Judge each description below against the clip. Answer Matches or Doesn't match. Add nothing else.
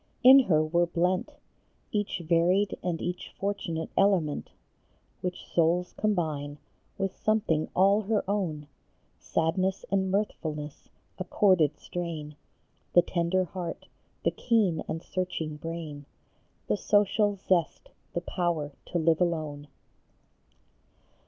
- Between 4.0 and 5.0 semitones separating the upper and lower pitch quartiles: Doesn't match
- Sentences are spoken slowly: Matches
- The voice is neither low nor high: Matches